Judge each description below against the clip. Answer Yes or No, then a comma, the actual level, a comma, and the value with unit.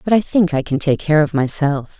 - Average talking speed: No, fast, 270 wpm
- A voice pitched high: No, medium, 155 Hz